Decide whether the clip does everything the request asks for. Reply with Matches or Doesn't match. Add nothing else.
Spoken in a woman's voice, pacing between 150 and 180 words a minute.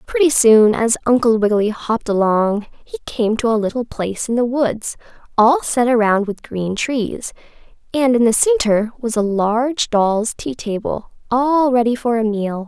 Matches